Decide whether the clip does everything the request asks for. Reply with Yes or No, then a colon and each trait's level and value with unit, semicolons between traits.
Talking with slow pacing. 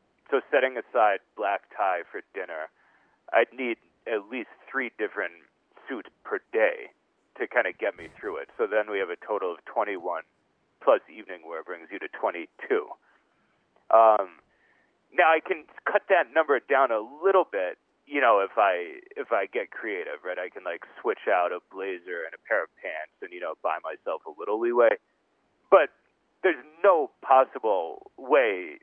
No: average, 175 wpm